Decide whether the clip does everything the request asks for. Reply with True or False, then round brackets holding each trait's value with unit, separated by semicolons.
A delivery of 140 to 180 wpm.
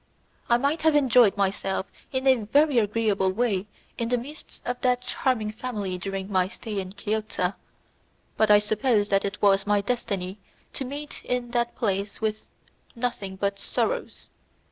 True (160 wpm)